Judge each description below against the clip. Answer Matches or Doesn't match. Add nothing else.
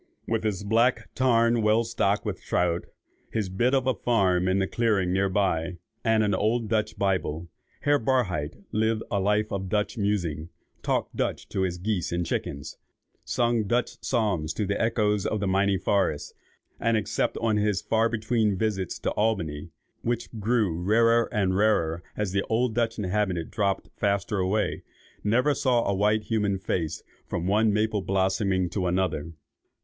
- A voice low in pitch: Matches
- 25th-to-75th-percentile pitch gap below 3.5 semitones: Matches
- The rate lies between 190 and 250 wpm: Doesn't match